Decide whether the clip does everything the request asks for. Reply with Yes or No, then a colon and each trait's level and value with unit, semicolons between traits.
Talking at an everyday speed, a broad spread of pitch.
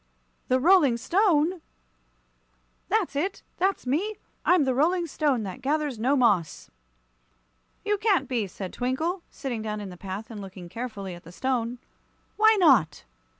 Yes: average, 150 wpm; wide, 8.2 semitones